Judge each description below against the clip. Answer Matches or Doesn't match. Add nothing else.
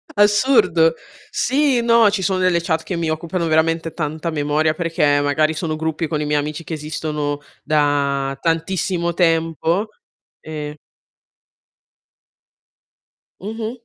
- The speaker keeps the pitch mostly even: Doesn't match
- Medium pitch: Matches